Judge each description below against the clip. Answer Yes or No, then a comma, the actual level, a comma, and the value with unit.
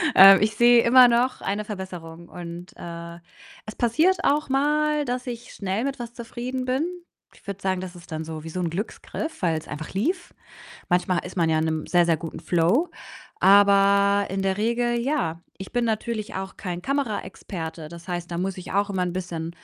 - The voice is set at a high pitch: Yes, high, 195 Hz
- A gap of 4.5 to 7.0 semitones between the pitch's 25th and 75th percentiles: Yes, wide, 5.6 semitones